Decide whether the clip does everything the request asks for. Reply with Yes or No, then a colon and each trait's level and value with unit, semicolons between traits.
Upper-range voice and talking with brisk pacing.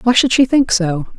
Yes: high, 225 Hz; fast, 255 wpm